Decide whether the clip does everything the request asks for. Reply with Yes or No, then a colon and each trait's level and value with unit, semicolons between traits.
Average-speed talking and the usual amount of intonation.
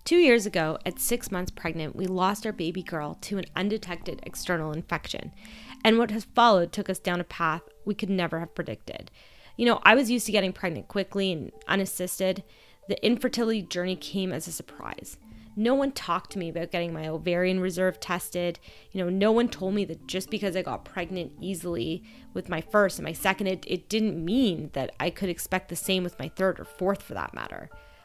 No: fast, 210 wpm; average, 3.4 semitones